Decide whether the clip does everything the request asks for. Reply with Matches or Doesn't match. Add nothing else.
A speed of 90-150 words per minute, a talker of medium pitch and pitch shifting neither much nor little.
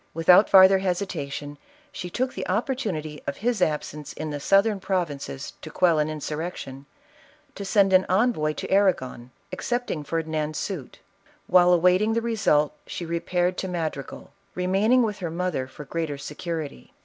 Doesn't match